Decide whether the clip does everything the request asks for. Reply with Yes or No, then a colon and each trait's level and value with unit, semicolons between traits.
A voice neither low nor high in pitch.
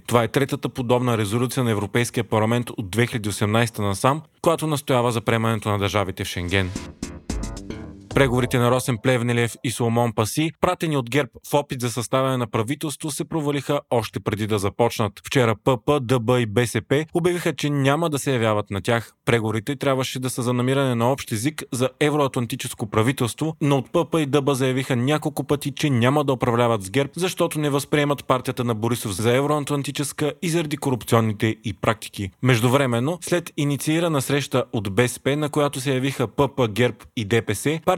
No: low, 130 Hz